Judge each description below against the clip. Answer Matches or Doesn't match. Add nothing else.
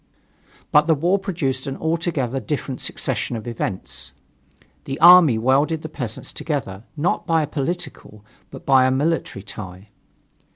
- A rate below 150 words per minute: Matches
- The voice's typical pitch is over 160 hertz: Doesn't match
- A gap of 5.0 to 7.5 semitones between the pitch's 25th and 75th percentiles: Matches